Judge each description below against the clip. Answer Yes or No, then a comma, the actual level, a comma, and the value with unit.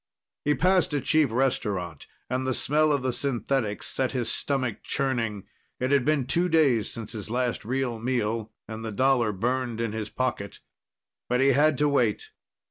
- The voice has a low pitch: Yes, low, 125 Hz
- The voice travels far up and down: No, average, 3.5 semitones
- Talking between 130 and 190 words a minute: Yes, average, 175 wpm